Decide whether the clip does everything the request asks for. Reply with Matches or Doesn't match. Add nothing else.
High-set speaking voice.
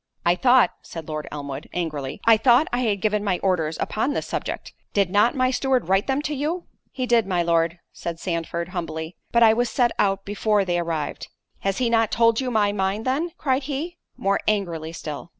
Matches